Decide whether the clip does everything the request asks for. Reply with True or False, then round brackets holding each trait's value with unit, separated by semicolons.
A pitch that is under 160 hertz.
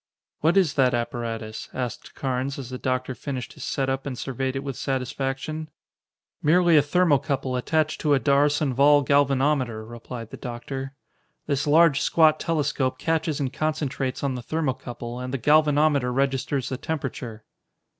True (135 Hz)